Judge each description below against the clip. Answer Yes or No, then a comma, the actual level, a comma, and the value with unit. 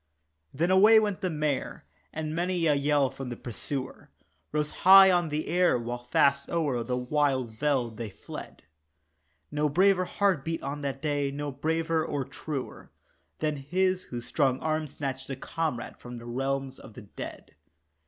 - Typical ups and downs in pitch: Yes, average, 3.7 semitones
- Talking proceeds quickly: No, average, 160 wpm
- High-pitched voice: No, medium, 145 Hz